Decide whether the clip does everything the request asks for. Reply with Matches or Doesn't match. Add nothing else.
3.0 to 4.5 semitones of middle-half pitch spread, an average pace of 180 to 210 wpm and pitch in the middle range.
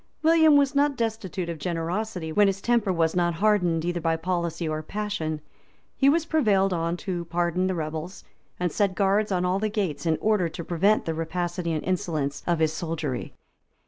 Matches